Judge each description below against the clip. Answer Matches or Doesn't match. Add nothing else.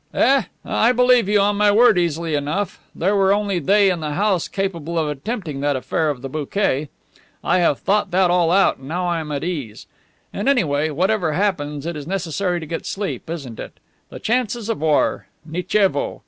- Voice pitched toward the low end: Doesn't match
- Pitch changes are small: Doesn't match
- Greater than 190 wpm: Matches